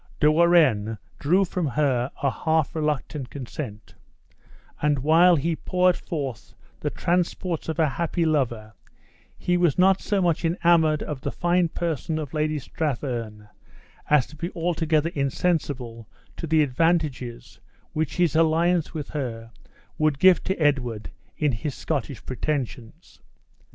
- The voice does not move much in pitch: No, average, 4.2 semitones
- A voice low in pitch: No, medium, 155 Hz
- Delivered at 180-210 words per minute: No, slow, 135 wpm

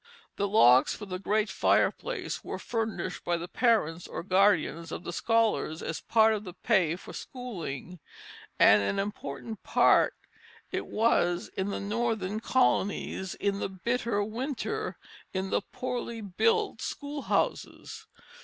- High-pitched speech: Yes, high, 205 Hz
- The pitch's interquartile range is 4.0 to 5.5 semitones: Yes, average, 4.3 semitones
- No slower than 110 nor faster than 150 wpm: Yes, average, 140 wpm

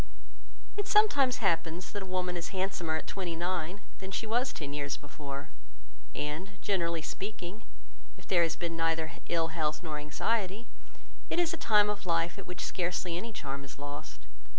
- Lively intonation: No, average, 3.9 semitones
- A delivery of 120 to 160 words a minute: No, average, 175 wpm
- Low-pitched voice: No, medium, 175 Hz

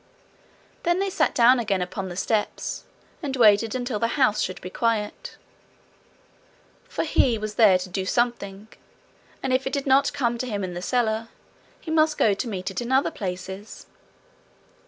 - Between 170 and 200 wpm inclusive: Yes, average, 175 wpm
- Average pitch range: Yes, average, 4.6 semitones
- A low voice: No, high, 225 Hz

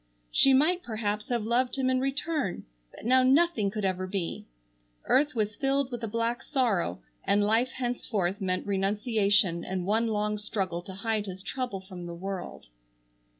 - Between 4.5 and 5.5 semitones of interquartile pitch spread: Yes, average, 4.8 semitones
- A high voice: Yes, high, 210 Hz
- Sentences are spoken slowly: No, average, 165 wpm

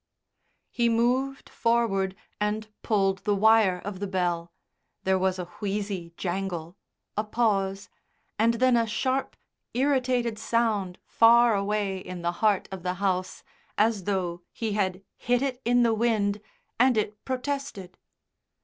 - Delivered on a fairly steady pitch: No, average, 3.6 semitones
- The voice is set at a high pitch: Yes, high, 210 Hz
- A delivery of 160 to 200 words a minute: No, average, 140 wpm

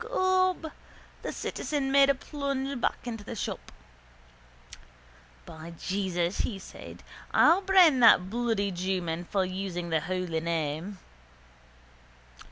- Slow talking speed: Yes, slow, 115 wpm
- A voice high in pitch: Yes, high, 200 Hz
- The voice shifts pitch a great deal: Yes, wide, 7.8 semitones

